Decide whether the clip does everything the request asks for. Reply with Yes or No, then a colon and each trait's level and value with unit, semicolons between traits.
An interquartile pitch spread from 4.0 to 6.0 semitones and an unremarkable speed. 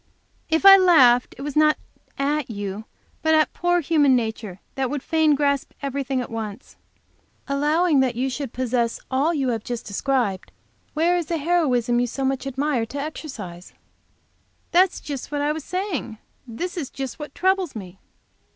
Yes: average, 4.4 semitones; average, 170 wpm